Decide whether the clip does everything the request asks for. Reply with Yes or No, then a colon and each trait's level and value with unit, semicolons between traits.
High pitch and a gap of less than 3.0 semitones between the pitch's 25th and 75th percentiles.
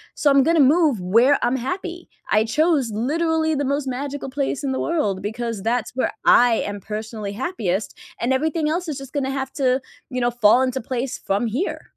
No: very high, 260 Hz; average, 4.4 semitones